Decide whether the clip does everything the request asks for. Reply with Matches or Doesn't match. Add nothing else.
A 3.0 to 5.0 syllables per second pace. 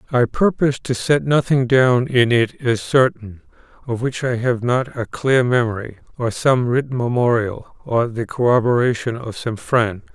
Matches